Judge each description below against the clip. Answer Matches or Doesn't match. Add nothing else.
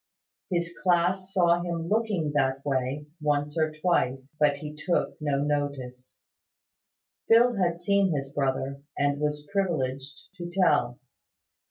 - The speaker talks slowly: Matches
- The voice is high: Doesn't match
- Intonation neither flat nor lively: Matches